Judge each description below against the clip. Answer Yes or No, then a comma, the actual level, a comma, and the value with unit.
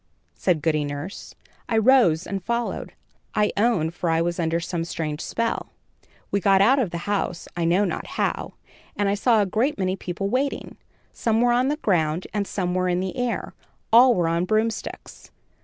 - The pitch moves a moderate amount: Yes, average, 5.0 semitones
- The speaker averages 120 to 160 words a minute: No, average, 190 wpm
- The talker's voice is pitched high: Yes, high, 195 Hz